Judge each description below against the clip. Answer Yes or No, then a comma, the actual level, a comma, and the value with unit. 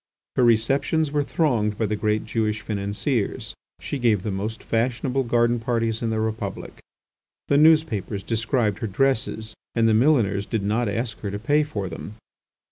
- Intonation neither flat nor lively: Yes, average, 3.1 semitones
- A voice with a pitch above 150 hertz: No, low, 115 Hz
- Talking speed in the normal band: Yes, average, 165 wpm